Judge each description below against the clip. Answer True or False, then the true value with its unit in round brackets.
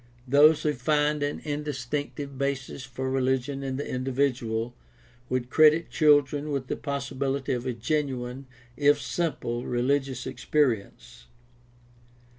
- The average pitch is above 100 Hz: True (135 Hz)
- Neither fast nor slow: False (120 wpm)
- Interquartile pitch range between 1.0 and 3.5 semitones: True (2.4 semitones)